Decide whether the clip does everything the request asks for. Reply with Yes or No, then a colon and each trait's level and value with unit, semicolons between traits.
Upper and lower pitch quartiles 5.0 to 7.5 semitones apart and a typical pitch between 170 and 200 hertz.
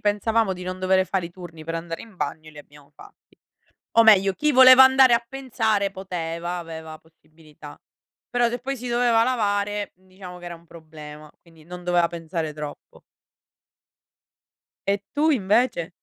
Yes: wide, 5.5 semitones; medium, 185 Hz